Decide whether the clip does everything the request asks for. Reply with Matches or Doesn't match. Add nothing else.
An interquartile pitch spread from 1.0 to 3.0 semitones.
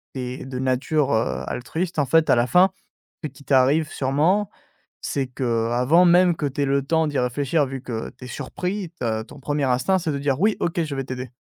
Doesn't match